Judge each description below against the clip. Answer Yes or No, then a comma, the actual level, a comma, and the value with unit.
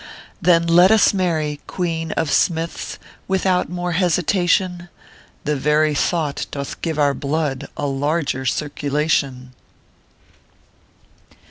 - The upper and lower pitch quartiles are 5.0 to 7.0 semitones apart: No, average, 3.3 semitones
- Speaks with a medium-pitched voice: Yes, medium, 160 Hz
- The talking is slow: Yes, slow, 105 wpm